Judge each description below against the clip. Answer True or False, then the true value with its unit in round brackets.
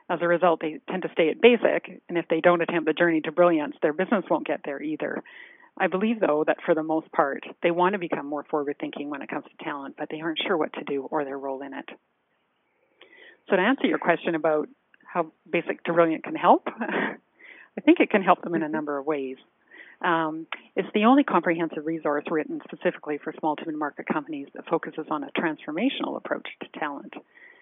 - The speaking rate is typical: False (220 wpm)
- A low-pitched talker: False (170 Hz)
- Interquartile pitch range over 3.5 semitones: True (5.0 semitones)